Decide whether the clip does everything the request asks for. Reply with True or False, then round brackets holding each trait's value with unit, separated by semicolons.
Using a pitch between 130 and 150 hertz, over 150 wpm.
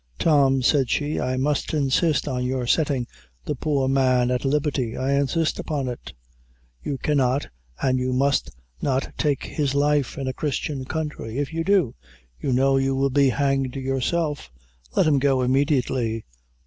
True (135 Hz; 160 wpm)